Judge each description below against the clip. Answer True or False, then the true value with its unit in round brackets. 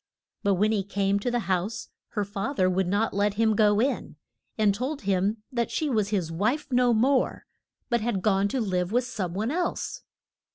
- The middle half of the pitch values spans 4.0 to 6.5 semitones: False (3.5 semitones)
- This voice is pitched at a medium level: False (210 Hz)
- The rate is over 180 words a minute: True (200 wpm)